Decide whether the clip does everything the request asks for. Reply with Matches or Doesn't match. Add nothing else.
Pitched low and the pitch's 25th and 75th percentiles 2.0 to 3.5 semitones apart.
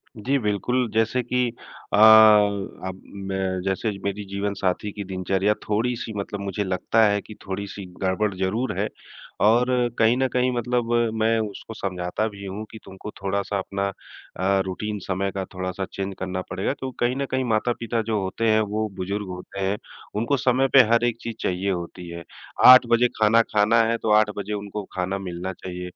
Matches